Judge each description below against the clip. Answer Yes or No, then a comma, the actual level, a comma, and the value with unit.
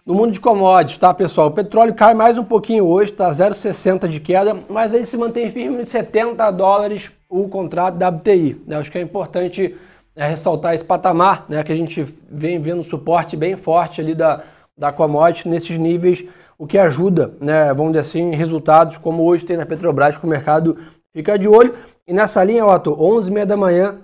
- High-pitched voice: No, medium, 180 Hz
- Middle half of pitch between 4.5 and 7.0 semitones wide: No, average, 4.0 semitones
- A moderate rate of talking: No, fast, 200 wpm